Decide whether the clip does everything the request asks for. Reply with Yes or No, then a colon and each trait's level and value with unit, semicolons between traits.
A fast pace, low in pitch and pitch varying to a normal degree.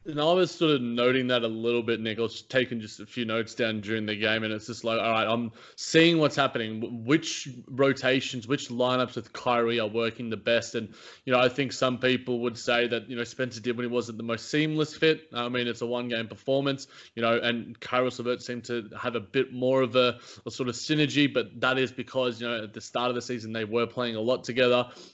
No: fast, 250 wpm; low, 120 Hz; narrow, 1.9 semitones